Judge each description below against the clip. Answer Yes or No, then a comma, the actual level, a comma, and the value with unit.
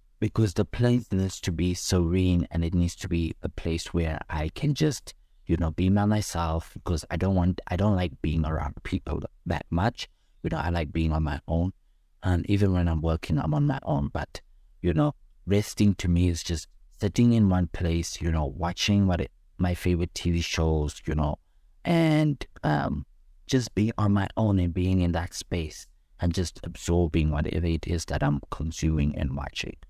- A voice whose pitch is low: Yes, very low, 85 Hz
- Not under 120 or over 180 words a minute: No, average, 195 wpm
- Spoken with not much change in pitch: No, average, 3.2 semitones